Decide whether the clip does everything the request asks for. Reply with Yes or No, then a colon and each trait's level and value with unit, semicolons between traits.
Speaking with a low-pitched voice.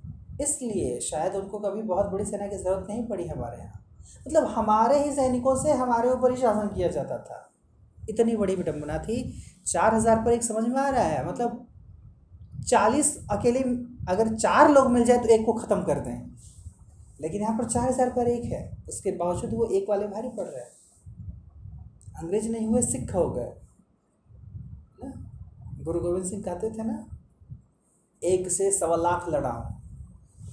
No: high, 205 Hz